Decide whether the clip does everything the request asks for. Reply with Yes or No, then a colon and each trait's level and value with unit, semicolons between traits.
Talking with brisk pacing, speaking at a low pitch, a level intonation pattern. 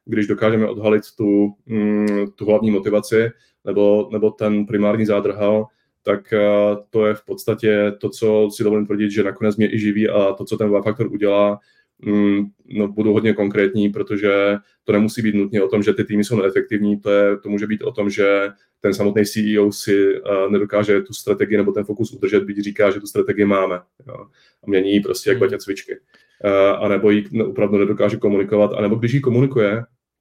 Yes: fast, 185 wpm; low, 105 Hz; narrow, 1.0 semitones